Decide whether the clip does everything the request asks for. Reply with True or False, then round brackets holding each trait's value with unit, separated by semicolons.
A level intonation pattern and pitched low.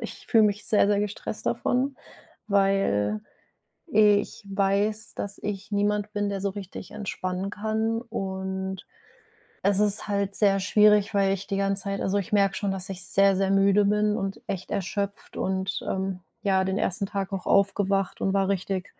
False (1.3 semitones; 200 Hz)